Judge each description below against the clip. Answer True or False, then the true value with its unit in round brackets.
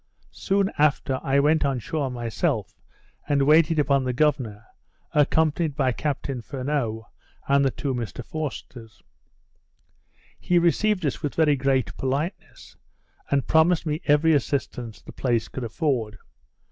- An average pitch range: True (3.6 semitones)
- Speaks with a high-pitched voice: False (140 Hz)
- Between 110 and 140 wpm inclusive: True (135 wpm)